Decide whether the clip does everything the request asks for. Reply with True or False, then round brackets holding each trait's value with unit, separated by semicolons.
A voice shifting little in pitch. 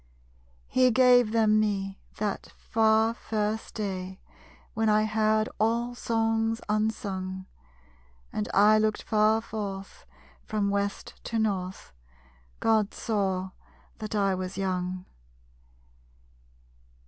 True (2.2 semitones)